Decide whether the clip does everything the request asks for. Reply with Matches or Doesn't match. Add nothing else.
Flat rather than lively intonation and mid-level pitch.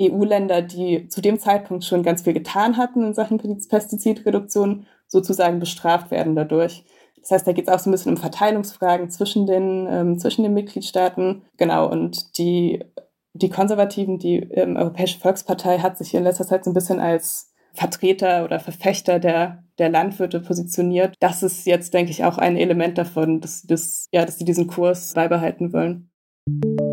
Matches